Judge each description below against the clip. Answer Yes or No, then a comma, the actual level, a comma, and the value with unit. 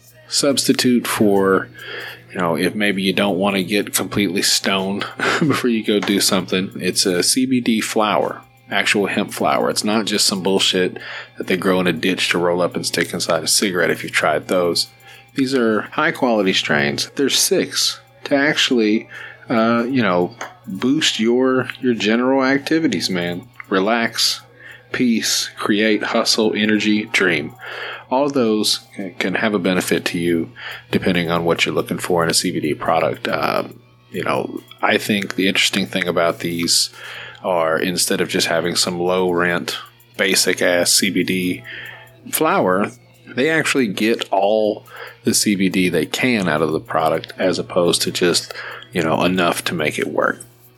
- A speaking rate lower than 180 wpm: Yes, average, 160 wpm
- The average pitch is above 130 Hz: No, low, 105 Hz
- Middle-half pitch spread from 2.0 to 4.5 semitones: No, average, 4.9 semitones